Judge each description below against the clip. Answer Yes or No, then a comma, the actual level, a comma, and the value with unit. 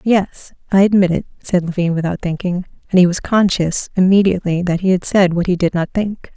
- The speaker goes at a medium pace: No, fast, 210 wpm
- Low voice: No, medium, 185 Hz